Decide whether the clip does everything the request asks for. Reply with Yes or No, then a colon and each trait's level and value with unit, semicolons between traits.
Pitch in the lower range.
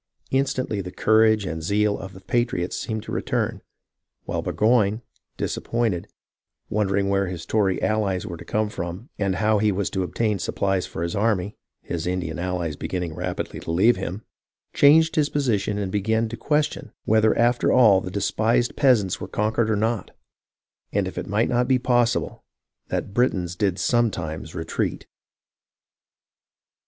Yes: low, 105 Hz